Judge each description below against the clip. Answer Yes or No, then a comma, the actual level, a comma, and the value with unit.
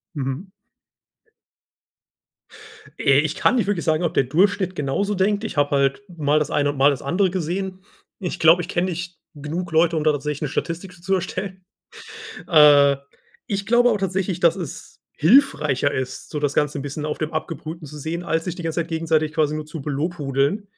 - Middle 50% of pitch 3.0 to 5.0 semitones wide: Yes, average, 3.7 semitones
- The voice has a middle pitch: Yes, medium, 160 Hz